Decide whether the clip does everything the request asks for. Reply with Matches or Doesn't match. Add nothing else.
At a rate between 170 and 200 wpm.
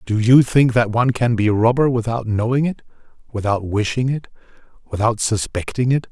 Matches